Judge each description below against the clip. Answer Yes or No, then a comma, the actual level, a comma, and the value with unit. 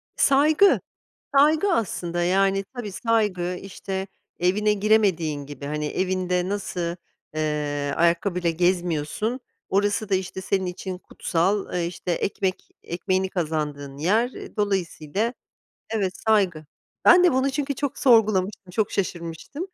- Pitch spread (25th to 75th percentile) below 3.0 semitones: No, average, 3.8 semitones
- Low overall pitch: No, high, 190 Hz